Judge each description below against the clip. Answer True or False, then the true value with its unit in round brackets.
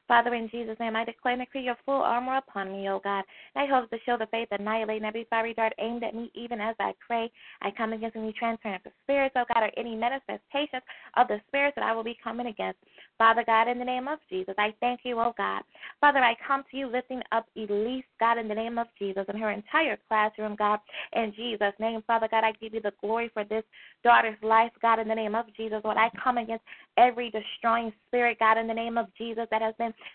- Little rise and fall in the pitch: True (1.7 semitones)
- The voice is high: True (230 Hz)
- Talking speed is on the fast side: True (240 wpm)